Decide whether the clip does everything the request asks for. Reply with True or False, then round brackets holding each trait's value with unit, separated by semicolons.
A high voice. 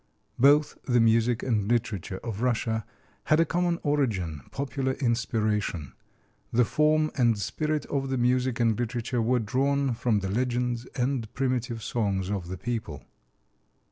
False (120 Hz)